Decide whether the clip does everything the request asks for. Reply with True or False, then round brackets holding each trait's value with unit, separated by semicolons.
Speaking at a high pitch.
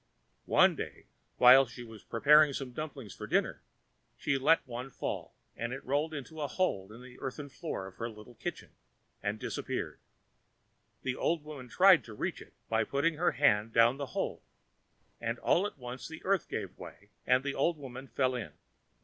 False (130 Hz)